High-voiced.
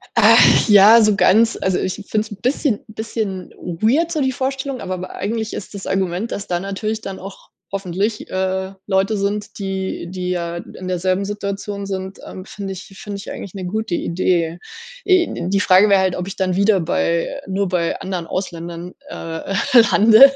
Yes: high, 195 Hz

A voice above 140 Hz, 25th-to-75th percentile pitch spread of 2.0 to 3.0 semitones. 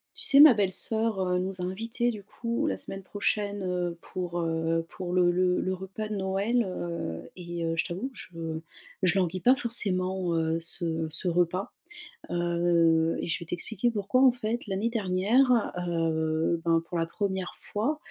No: medium, 185 Hz; average, 3.7 semitones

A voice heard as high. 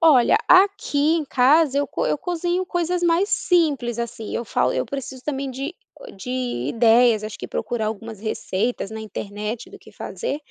Yes: very high, 260 Hz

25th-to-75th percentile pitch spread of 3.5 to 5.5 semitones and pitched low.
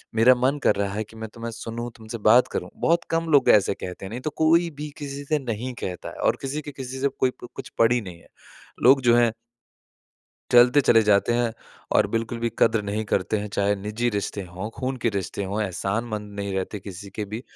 Yes: average, 3.8 semitones; low, 115 Hz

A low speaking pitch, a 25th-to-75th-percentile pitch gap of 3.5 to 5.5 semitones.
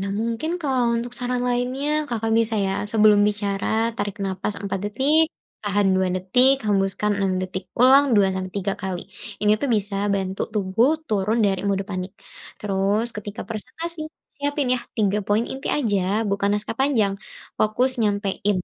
No: high, 210 Hz; average, 3.8 semitones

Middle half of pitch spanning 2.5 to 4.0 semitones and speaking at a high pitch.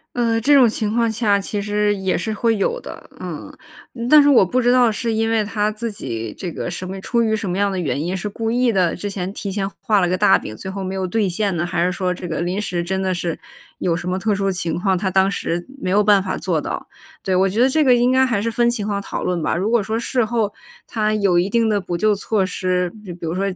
Yes: average, 3.5 semitones; high, 200 Hz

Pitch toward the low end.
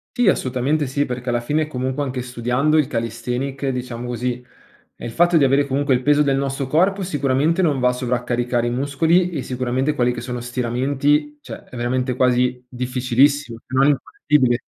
Yes: low, 130 Hz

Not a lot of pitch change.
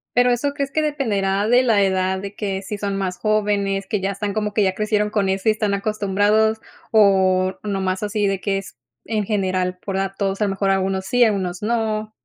Yes: narrow, 1.9 semitones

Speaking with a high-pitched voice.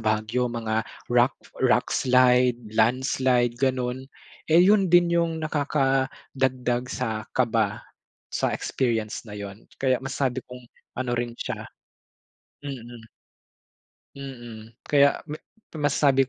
No: low, 125 Hz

